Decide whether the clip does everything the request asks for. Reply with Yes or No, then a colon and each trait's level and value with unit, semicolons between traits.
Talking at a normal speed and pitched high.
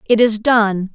Yes: average, 190 wpm; high, 215 Hz